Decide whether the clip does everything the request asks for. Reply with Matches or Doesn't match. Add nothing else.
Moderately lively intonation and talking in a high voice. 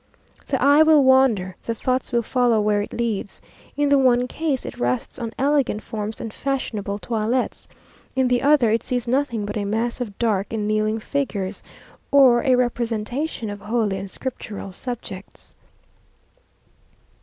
Matches